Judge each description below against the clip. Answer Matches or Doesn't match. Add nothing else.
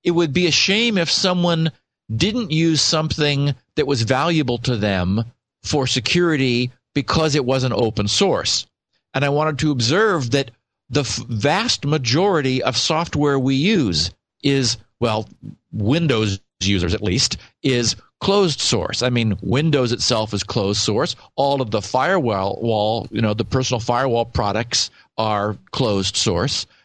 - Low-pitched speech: Matches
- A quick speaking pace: Doesn't match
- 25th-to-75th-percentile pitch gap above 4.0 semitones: Matches